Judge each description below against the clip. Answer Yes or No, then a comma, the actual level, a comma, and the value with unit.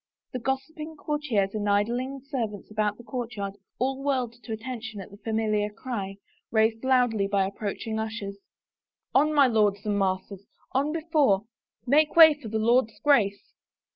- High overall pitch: Yes, high, 225 Hz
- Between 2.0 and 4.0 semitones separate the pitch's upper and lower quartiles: No, average, 4.4 semitones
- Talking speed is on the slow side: No, average, 160 wpm